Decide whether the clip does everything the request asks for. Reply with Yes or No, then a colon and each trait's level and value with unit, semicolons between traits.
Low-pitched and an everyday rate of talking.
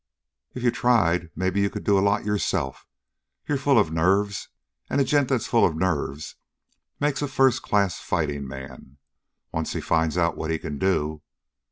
Yes: very low, 95 Hz; average, 180 wpm